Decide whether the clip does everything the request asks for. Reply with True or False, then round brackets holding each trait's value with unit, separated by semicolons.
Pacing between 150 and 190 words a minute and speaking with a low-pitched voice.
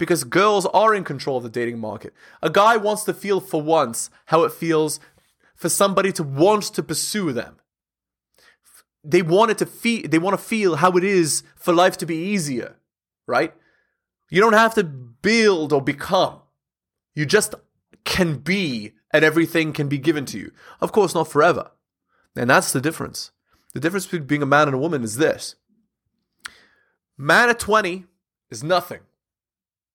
False (170 wpm; 165 Hz)